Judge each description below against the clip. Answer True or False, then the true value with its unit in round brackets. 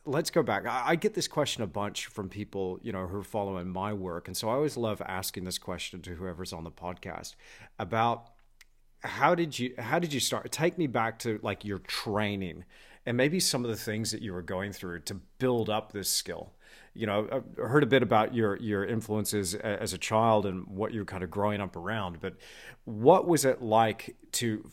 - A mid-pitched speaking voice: False (110 Hz)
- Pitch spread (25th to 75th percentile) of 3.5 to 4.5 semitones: True (3.8 semitones)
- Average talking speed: False (215 wpm)